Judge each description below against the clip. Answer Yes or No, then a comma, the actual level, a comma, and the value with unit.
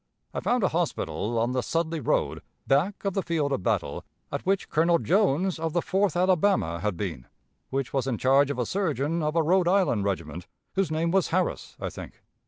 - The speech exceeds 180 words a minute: Yes, average, 200 wpm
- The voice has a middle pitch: Yes, medium, 160 Hz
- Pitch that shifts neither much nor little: No, wide, 6.2 semitones